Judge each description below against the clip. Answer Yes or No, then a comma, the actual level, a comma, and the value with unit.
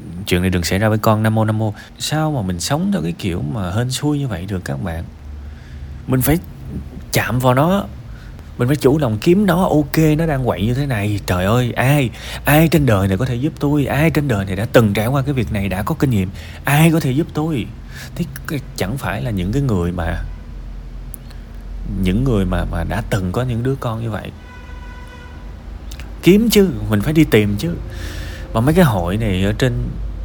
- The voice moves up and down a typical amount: No, wide, 7.6 semitones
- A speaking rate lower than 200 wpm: No, average, 215 wpm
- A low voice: Yes, low, 110 Hz